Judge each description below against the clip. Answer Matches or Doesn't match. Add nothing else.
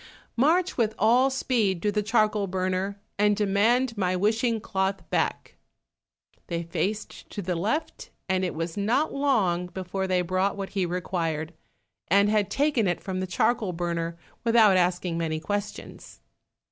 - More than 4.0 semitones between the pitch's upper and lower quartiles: Doesn't match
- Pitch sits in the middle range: Doesn't match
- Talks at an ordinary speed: Matches